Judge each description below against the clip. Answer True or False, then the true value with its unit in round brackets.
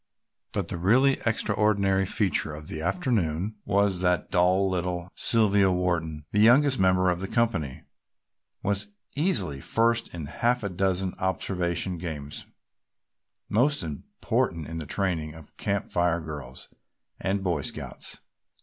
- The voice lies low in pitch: True (95 Hz)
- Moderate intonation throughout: True (3.8 semitones)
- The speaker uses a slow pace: True (130 wpm)